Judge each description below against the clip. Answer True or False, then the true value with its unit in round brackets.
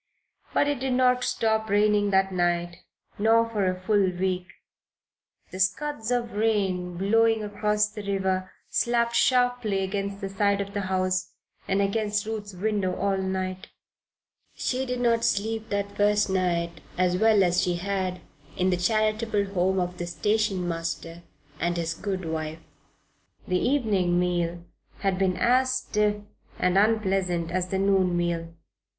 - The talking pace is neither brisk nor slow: True (150 wpm)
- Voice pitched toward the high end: True (195 Hz)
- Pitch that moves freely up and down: False (3.0 semitones)